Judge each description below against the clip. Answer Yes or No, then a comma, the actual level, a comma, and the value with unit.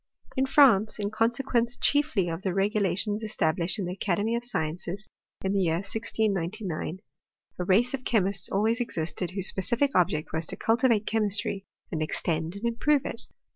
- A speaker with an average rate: Yes, average, 165 wpm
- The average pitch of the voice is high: Yes, high, 200 Hz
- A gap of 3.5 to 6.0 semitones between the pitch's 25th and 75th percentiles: Yes, average, 4.4 semitones